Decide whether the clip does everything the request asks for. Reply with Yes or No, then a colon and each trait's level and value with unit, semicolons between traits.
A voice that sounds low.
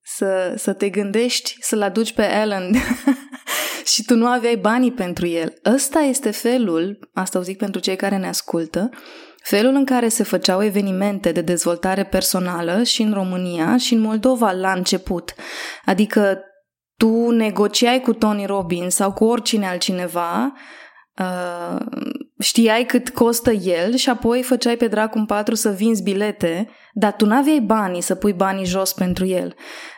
No: high, 215 Hz